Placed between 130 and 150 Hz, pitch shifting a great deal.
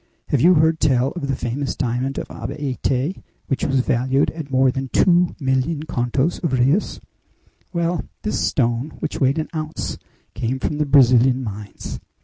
No: low, 135 Hz; average, 3.5 semitones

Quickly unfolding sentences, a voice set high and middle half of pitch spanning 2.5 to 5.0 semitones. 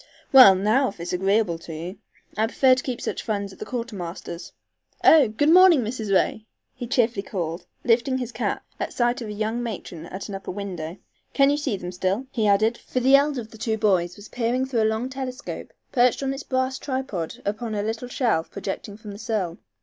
Yes: fast, 210 wpm; high, 220 Hz; average, 4.5 semitones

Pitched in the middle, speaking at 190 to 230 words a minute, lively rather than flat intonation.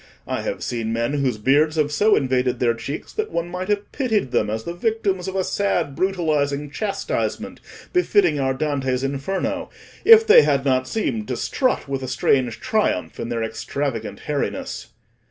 No: medium, 145 Hz; average, 170 wpm; wide, 7.1 semitones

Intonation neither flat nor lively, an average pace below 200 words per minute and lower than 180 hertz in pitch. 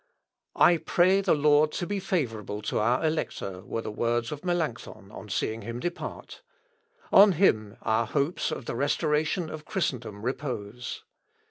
No: wide, 7.0 semitones; average, 150 wpm; medium, 140 Hz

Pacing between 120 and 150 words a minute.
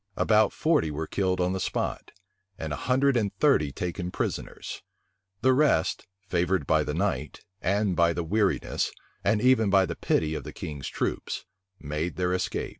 No: average, 170 wpm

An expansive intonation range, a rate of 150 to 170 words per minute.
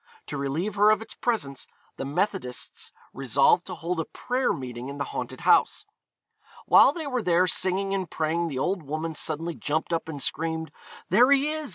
No: wide, 6.0 semitones; average, 185 wpm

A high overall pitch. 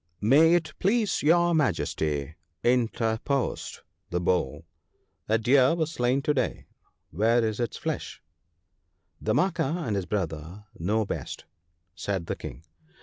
No: low, 115 Hz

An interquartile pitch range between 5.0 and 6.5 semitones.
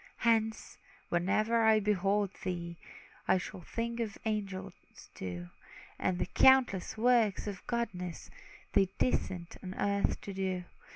No: average, 3.3 semitones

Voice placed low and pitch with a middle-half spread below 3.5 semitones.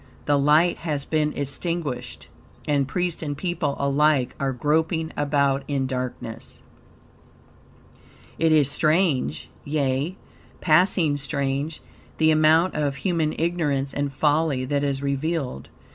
No: medium, 145 Hz; narrow, 2.6 semitones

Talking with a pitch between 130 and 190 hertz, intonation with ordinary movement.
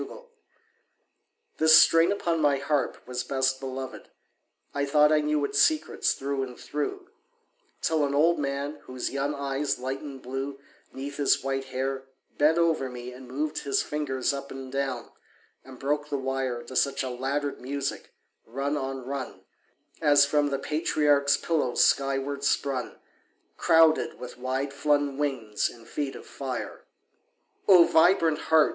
No: medium, 140 Hz; narrow, 1.9 semitones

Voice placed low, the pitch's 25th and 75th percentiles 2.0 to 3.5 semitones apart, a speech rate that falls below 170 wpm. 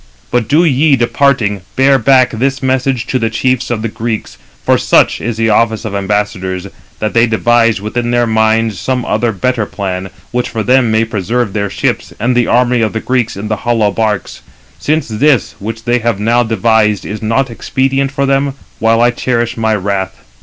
No: low, 115 Hz; average, 2.8 semitones; average, 190 wpm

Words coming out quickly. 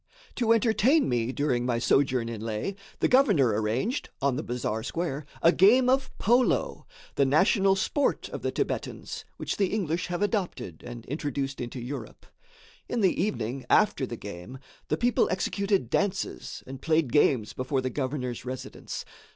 No: average, 160 wpm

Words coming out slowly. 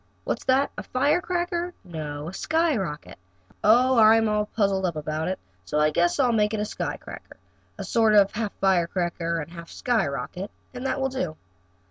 No: average, 175 wpm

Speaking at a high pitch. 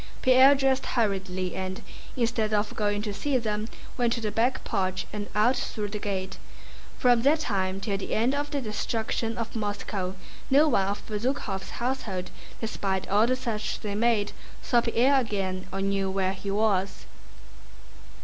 Yes: high, 215 Hz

